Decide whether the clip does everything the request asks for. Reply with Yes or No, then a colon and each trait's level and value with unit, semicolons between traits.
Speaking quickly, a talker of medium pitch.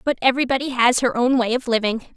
No: fast, 220 wpm; high, 245 Hz